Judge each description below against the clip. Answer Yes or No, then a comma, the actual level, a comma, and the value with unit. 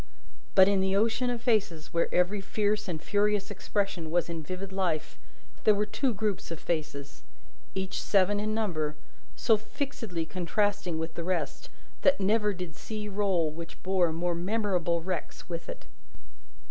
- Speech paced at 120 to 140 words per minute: No, average, 160 wpm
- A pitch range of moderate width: Yes, average, 3.7 semitones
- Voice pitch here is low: No, high, 190 Hz